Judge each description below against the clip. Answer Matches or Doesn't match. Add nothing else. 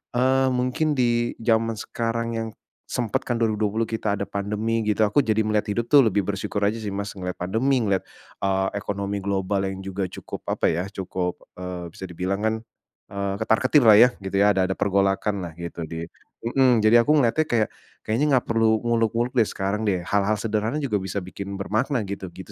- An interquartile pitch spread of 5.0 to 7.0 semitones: Doesn't match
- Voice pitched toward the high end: Doesn't match